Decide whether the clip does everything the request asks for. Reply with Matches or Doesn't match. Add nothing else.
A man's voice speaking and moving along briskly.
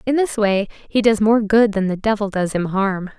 Doesn't match